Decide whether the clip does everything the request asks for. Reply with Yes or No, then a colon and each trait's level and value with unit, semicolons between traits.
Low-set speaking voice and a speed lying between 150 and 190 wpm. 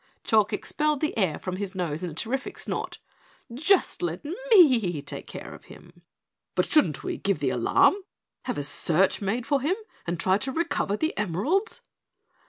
No: high, 205 Hz; average, 175 wpm